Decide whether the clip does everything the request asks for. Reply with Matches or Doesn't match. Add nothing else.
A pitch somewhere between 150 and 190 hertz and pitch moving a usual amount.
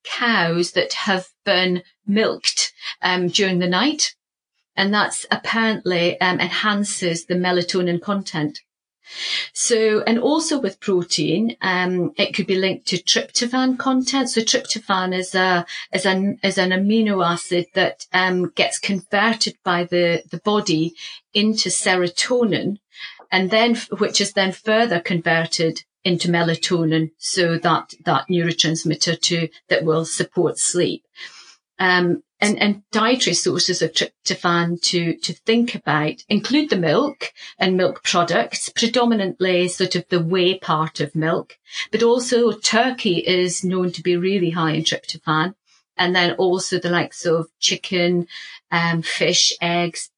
Matches